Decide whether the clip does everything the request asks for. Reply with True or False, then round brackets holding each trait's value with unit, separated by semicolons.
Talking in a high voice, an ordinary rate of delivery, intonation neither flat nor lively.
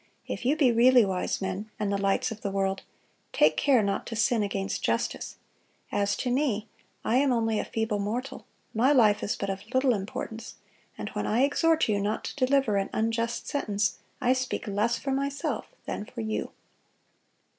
True (225 Hz; 185 wpm; 4.1 semitones)